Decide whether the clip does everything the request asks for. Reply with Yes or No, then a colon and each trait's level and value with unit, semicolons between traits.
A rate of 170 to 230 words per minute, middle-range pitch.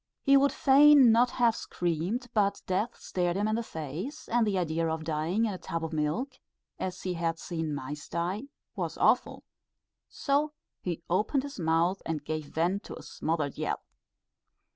Yes: average, 175 wpm; medium, 180 Hz